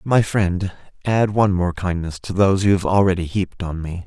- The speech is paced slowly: No, fast, 205 wpm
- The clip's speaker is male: Yes, male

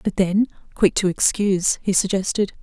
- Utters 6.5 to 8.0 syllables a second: No, 5.1 syllables/s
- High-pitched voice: Yes, high, 195 Hz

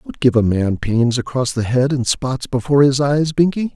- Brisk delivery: Yes, fast, 225 wpm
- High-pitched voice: No, low, 130 Hz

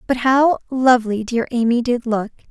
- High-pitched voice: Yes, high, 240 Hz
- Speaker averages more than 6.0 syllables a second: No, 5.0 syllables/s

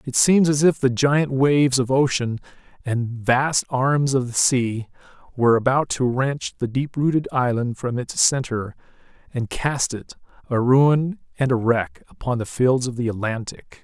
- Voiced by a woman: No, male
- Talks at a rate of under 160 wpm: No, average, 175 wpm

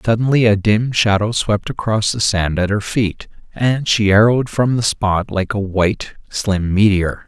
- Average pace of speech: Yes, average, 180 wpm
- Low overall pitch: Yes, low, 105 Hz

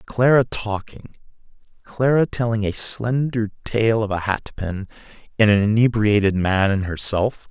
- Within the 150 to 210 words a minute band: No, slow, 135 wpm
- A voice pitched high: No, low, 110 Hz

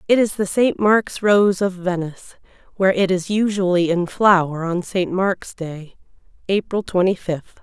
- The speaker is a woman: Yes, female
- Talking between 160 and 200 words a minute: Yes, average, 165 wpm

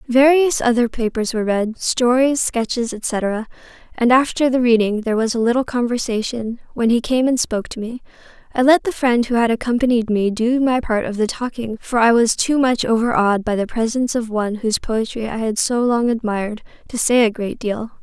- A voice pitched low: No, high, 235 Hz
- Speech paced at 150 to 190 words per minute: No, average, 200 wpm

